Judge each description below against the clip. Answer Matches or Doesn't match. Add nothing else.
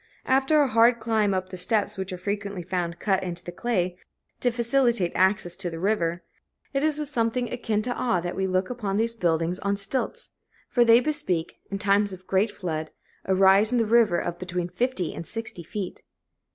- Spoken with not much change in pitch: Doesn't match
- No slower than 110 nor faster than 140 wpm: Doesn't match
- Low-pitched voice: Doesn't match